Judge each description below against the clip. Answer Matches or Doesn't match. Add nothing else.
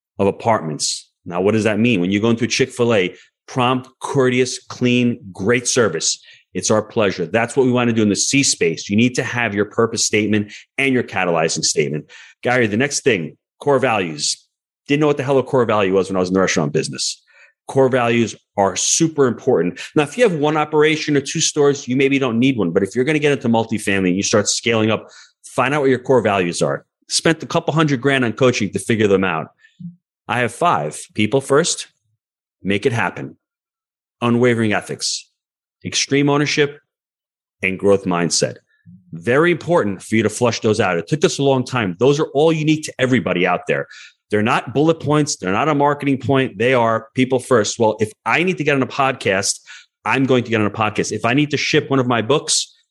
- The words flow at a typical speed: Doesn't match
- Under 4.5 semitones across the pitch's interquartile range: Doesn't match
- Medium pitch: Doesn't match